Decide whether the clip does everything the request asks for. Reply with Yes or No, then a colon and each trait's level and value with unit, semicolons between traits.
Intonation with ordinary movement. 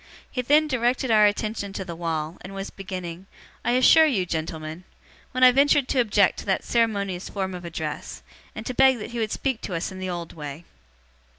No: wide, 5.9 semitones